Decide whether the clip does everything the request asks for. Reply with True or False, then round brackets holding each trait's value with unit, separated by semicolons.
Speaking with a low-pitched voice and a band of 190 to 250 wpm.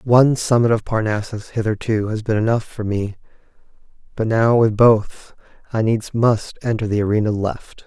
False (110 Hz; 160 wpm)